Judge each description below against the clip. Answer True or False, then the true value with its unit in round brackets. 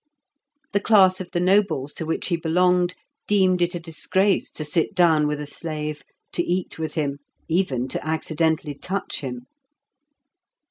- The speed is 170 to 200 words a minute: False (155 wpm)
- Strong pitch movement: False (3.3 semitones)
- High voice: False (165 Hz)